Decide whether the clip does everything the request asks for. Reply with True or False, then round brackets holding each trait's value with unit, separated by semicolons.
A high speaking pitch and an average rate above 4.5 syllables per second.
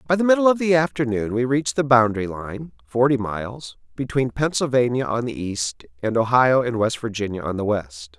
False (125 Hz; 5.4 syllables/s)